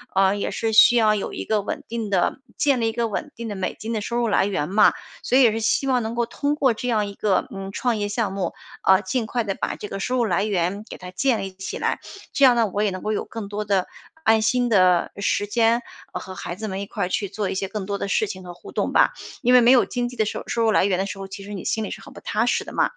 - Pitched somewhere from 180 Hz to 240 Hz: Yes, high, 210 Hz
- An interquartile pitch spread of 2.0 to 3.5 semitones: Yes, average, 3.2 semitones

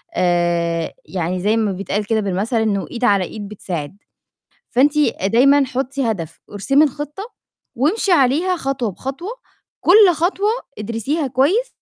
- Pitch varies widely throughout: Yes, wide, 6.8 semitones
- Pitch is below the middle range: No, high, 240 Hz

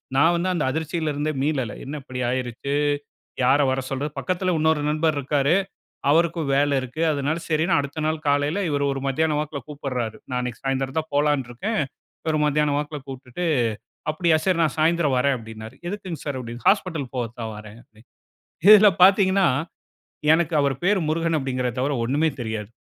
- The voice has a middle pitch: Yes, medium, 145 Hz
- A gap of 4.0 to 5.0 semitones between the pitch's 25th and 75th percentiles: No, average, 3.6 semitones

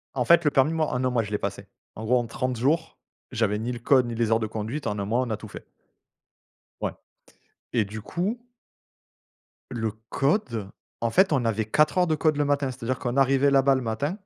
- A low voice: Yes, low, 125 Hz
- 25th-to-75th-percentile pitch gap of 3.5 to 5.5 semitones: Yes, average, 4.2 semitones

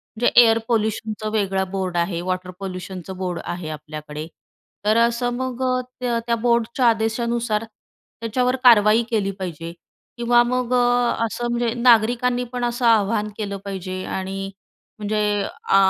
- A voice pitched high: Yes, high, 220 Hz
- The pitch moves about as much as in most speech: Yes, average, 3.9 semitones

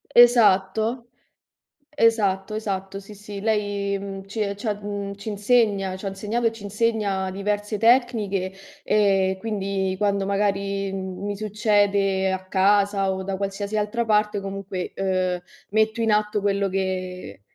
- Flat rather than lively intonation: Yes, narrow, 1.5 semitones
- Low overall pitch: No, high, 200 Hz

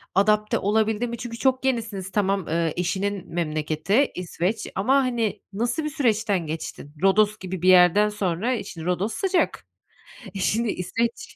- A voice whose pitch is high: Yes, high, 205 Hz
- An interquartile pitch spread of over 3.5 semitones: Yes, average, 4.3 semitones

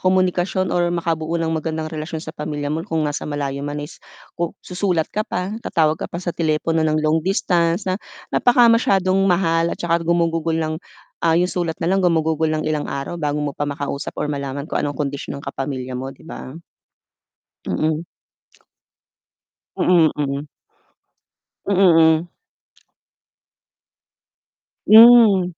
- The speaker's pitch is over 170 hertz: No, medium, 165 Hz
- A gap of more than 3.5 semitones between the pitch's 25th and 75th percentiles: No, average, 2.9 semitones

